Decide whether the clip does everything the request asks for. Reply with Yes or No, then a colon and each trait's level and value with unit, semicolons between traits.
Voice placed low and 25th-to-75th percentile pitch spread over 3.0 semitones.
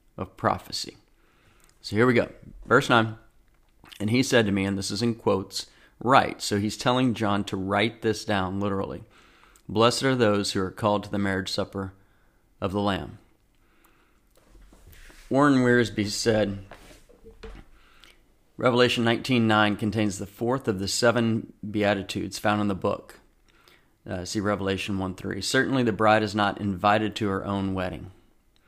No: low, 105 Hz; narrow, 2.5 semitones